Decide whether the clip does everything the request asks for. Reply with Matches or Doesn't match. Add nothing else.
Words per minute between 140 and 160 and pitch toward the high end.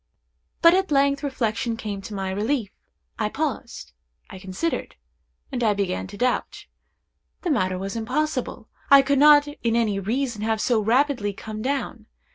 Matches